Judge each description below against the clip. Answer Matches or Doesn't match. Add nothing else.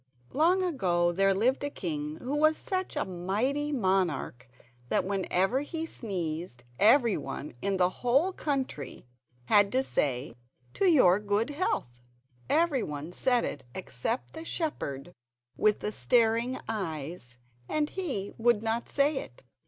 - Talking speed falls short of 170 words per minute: Matches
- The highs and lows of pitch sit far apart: Matches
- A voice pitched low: Doesn't match